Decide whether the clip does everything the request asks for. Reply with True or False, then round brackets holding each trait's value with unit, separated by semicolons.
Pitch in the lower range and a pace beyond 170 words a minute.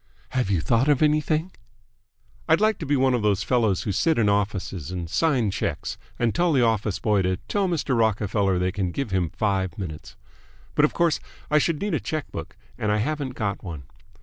True (110 Hz; 205 wpm)